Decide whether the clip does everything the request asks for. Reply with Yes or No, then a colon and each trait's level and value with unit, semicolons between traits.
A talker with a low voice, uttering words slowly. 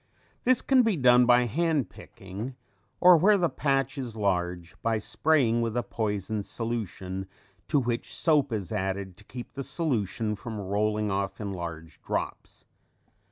No: low, 115 Hz; average, 155 wpm